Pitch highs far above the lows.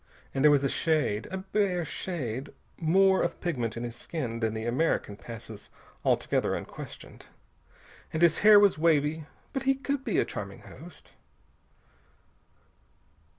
Yes: wide, 7.8 semitones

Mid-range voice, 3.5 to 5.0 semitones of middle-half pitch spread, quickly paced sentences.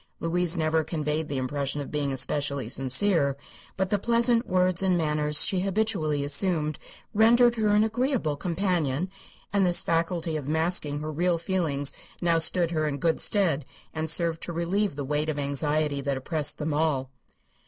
No: medium, 160 Hz; average, 3.9 semitones; average, 165 wpm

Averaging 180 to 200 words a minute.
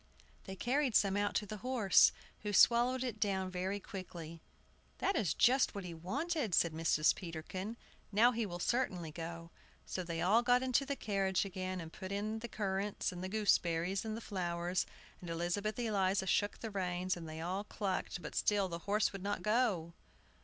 Yes: average, 185 wpm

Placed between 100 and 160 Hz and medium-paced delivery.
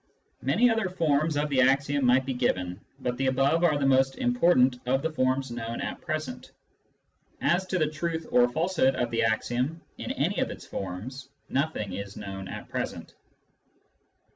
Yes: low, 135 Hz; average, 170 wpm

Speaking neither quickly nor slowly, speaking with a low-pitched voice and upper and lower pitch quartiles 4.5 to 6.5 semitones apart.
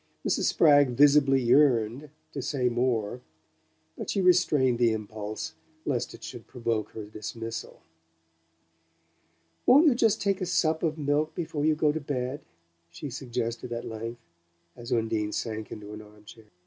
Yes: average, 150 wpm; low, 125 Hz; average, 4.9 semitones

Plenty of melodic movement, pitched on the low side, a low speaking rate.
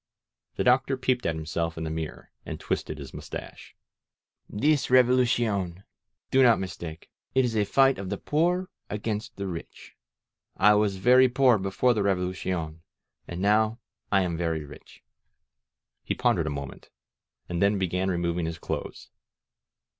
No: wide, 6.5 semitones; low, 100 Hz; average, 155 wpm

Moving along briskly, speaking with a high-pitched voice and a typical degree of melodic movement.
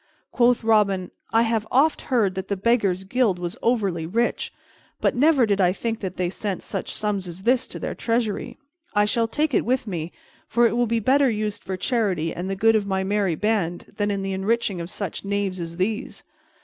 Yes: fast, 210 wpm; high, 205 Hz; average, 3.5 semitones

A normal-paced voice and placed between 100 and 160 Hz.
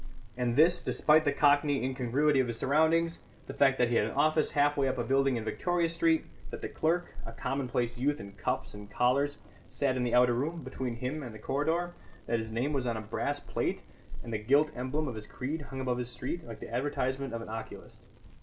No: fast, 225 wpm; low, 135 Hz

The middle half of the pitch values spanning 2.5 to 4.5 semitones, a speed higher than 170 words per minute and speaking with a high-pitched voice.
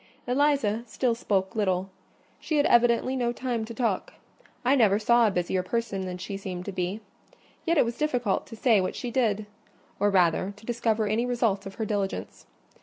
Yes: average, 3.6 semitones; average, 185 wpm; high, 220 Hz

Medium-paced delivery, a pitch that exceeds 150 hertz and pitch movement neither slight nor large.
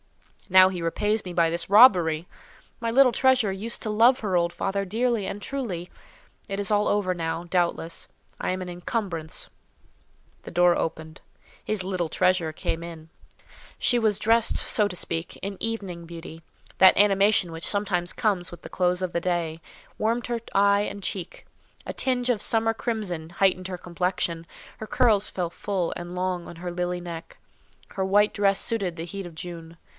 Yes: average, 170 wpm; medium, 185 Hz; average, 3.4 semitones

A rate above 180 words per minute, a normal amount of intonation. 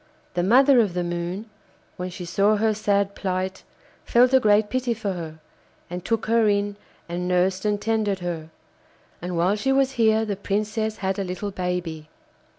No: average, 175 wpm; average, 3.4 semitones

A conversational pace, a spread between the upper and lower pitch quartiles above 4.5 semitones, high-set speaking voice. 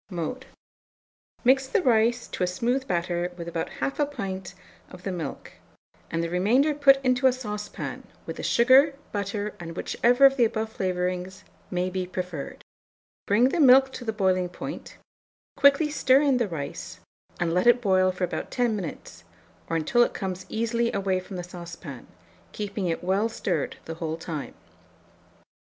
Yes: average, 165 wpm; wide, 5.6 semitones; high, 200 Hz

